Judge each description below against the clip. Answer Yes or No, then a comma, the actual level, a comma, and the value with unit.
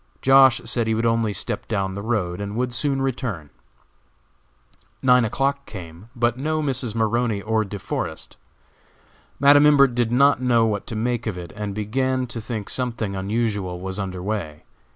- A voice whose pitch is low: Yes, low, 115 Hz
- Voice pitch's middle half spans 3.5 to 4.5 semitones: Yes, average, 3.9 semitones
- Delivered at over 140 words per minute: Yes, average, 170 wpm